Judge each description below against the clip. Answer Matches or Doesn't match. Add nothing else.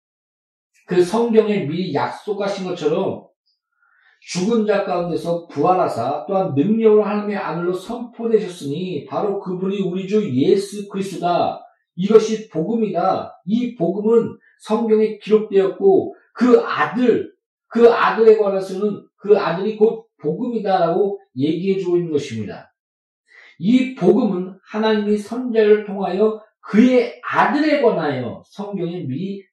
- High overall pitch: Matches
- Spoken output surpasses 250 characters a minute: Matches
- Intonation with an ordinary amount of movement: Matches